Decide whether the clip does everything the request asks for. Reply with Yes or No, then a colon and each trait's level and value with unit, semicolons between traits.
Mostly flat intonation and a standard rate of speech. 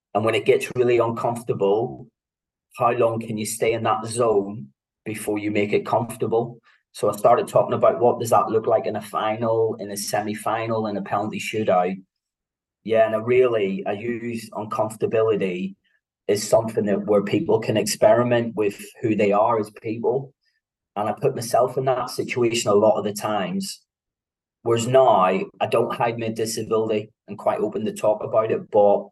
Yes: narrow, 2.2 semitones; average, 180 wpm